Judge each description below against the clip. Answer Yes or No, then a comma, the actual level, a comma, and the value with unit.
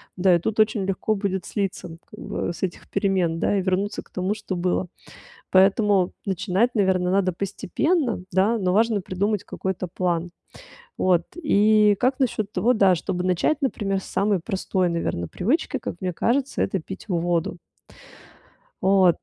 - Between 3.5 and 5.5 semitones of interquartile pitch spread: No, average, 2.7 semitones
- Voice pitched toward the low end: No, high, 190 Hz